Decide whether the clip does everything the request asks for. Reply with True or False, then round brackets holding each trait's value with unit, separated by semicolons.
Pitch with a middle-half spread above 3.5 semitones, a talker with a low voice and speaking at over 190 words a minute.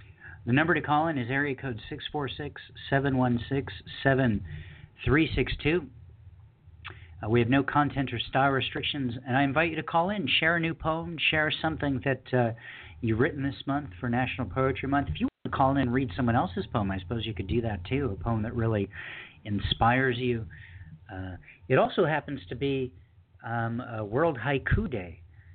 False (4.5 semitones; 125 Hz; 180 wpm)